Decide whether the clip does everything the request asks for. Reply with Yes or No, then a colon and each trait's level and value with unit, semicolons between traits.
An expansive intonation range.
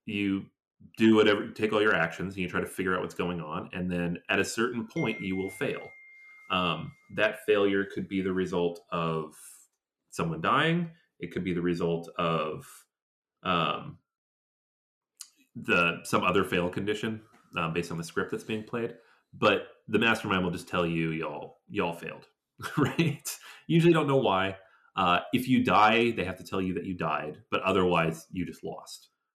No: average, 4.6 semitones